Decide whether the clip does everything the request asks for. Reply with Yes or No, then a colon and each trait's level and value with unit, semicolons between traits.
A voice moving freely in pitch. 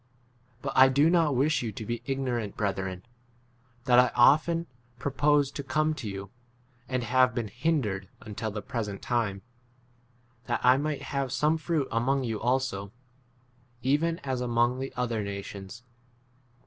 No: average, 4.3 semitones